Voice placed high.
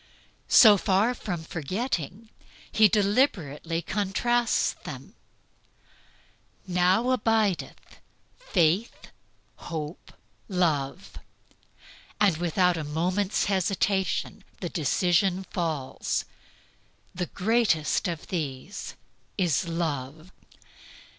No: medium, 180 Hz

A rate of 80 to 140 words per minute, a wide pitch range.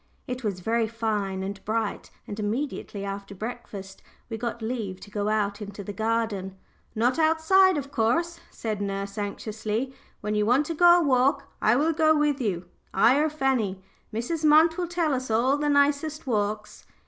No: average, 175 wpm; wide, 6.0 semitones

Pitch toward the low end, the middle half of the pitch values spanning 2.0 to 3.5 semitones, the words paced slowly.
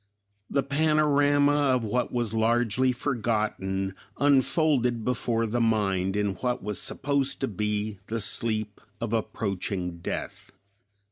No: low, 115 Hz; average, 4.3 semitones; slow, 120 wpm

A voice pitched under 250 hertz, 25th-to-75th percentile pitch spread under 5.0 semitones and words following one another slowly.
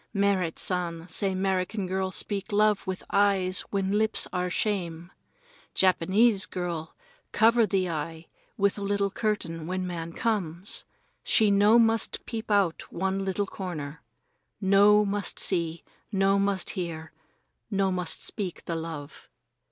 Yes: high, 190 Hz; average, 2.9 semitones; slow, 130 wpm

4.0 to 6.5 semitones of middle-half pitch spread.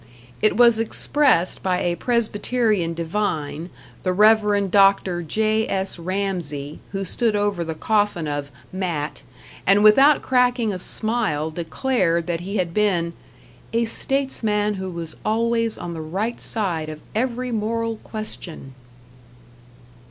Yes: average, 4.7 semitones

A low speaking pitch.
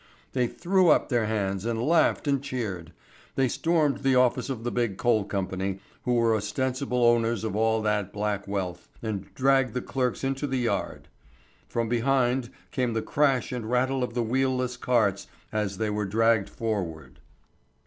Yes: low, 120 Hz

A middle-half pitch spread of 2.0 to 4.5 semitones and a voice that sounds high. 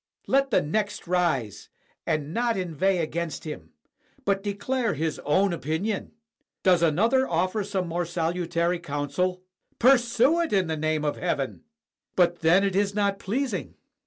No: average, 4.2 semitones; medium, 180 Hz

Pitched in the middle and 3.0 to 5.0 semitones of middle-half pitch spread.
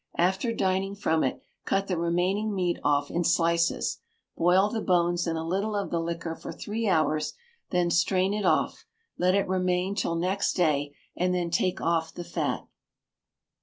No: medium, 180 Hz; narrow, 2.4 semitones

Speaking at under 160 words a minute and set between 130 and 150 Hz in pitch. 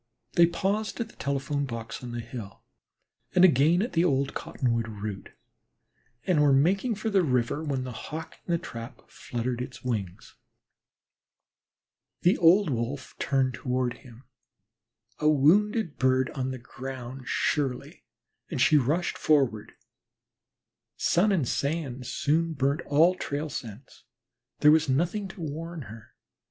Yes: average, 140 wpm; medium, 140 Hz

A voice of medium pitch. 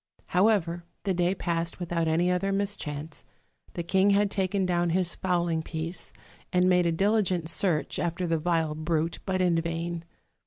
Yes: medium, 175 Hz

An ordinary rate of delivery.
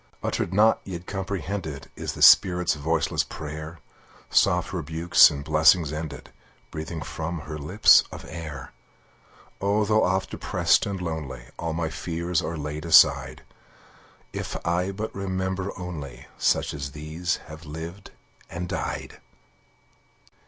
No: slow, 130 wpm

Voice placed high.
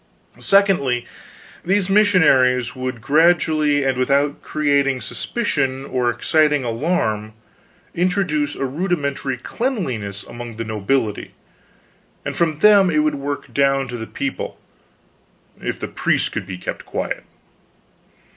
No: medium, 140 Hz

